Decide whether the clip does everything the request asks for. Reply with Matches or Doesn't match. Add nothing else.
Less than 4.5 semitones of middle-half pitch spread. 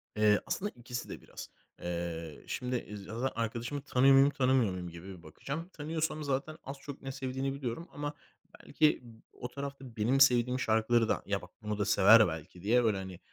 Doesn't match